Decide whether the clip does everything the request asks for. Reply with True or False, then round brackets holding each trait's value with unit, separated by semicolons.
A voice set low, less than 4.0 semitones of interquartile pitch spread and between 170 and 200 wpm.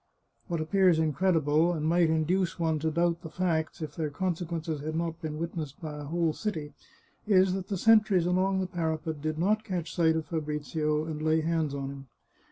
False (160 Hz; 2.4 semitones; 190 wpm)